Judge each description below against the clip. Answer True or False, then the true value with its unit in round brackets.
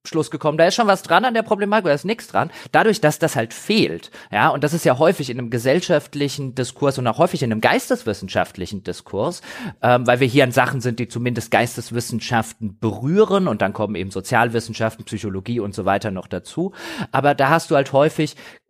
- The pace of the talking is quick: True (205 wpm)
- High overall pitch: False (135 Hz)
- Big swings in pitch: True (6.3 semitones)